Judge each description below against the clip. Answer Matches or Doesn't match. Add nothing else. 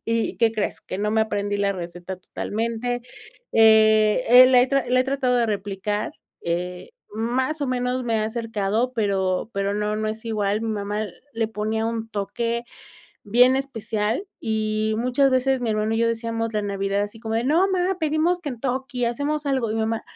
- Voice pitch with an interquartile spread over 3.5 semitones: Doesn't match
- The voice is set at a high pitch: Matches